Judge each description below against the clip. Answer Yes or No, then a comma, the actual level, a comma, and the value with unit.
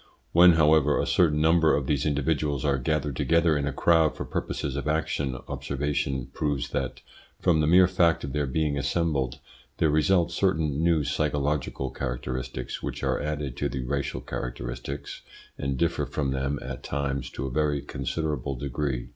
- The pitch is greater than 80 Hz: No, very low, 75 Hz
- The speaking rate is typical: Yes, average, 165 wpm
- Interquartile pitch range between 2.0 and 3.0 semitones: Yes, narrow, 2.6 semitones